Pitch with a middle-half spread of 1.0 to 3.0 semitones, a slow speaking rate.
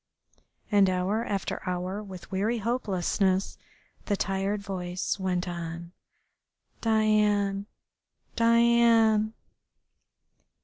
Yes: average, 2.7 semitones; slow, 80 wpm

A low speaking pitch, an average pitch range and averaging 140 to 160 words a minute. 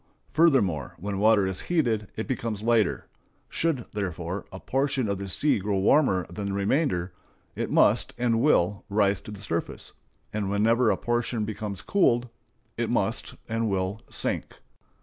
Yes: low, 105 Hz; average, 3.5 semitones; average, 155 wpm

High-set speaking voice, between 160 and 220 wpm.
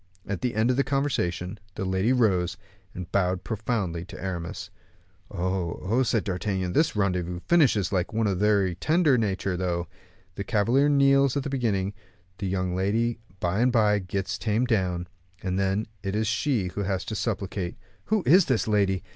No: low, 100 Hz; average, 180 wpm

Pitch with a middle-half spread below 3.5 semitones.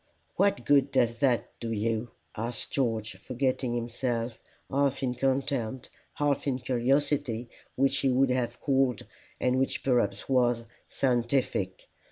Yes: narrow, 2.5 semitones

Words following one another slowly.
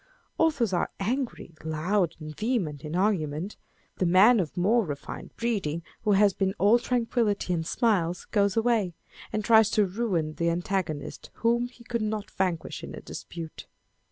No: average, 155 wpm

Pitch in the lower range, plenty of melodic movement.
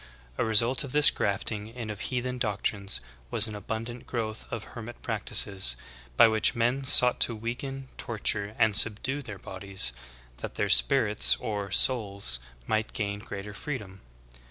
No: low, 110 Hz; average, 3.0 semitones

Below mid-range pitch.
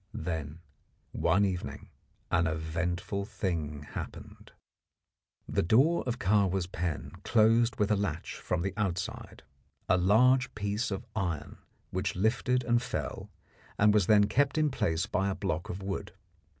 Yes: low, 100 Hz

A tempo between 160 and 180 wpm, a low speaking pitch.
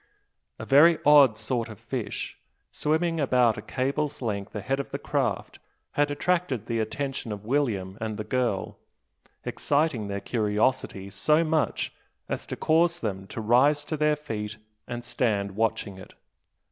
No: average, 150 wpm; low, 120 Hz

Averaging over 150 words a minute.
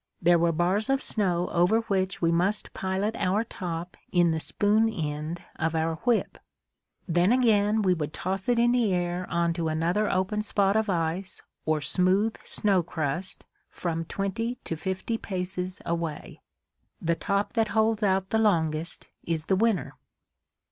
Yes: average, 160 wpm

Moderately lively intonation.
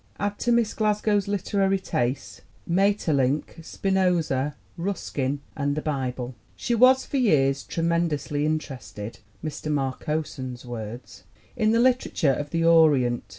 No: wide, 6.6 semitones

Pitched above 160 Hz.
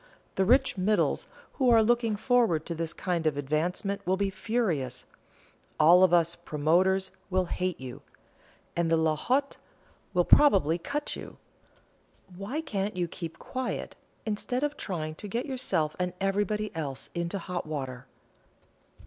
Yes: medium, 185 Hz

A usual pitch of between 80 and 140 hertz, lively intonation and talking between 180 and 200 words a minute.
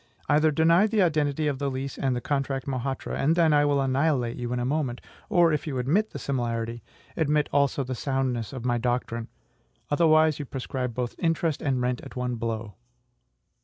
No: low, 135 Hz; average, 3.5 semitones; average, 190 wpm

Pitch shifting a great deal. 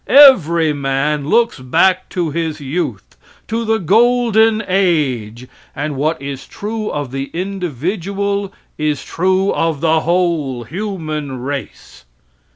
Yes: wide, 5.7 semitones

